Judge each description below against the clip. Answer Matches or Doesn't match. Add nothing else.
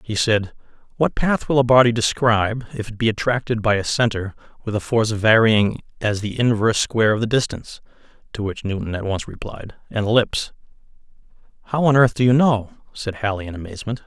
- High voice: Doesn't match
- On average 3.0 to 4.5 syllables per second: Doesn't match